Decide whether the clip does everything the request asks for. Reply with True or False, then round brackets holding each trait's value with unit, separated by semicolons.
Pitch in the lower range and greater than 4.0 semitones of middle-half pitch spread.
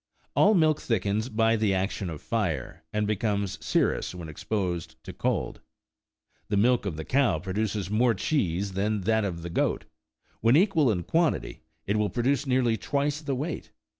True (105 Hz; 4.9 semitones)